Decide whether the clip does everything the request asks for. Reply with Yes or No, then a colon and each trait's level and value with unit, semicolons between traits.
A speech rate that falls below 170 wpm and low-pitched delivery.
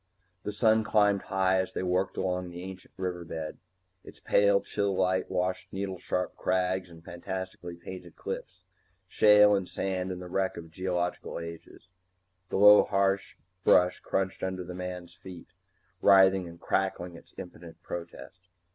Yes: average, 155 wpm; very low, 95 Hz